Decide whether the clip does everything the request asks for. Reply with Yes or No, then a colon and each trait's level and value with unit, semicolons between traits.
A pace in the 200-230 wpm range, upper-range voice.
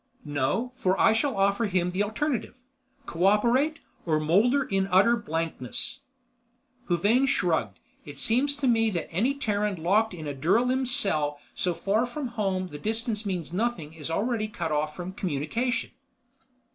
No: average, 145 wpm; high, 205 Hz